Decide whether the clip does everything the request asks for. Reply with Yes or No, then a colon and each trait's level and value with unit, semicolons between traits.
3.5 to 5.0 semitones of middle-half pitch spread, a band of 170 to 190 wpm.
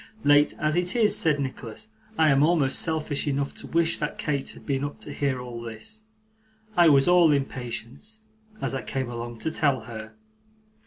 Yes: average, 4.0 semitones; average, 180 wpm